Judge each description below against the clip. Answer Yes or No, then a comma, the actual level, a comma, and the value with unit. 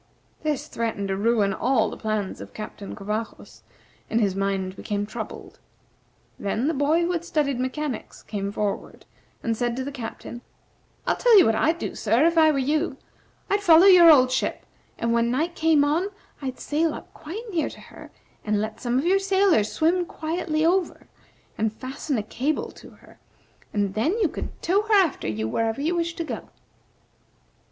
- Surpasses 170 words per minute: Yes, average, 185 wpm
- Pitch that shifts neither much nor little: No, wide, 7.2 semitones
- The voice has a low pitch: No, very high, 275 Hz